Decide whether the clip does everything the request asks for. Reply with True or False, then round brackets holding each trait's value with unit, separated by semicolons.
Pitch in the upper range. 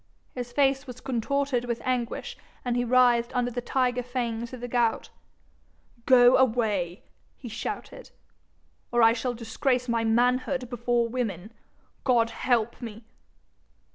True (245 Hz)